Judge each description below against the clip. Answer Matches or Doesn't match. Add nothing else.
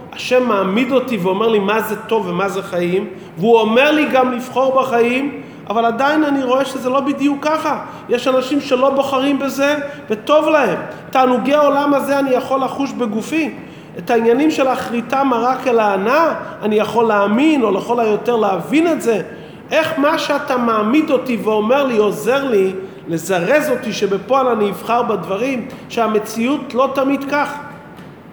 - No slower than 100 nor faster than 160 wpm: Matches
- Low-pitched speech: Doesn't match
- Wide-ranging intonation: Doesn't match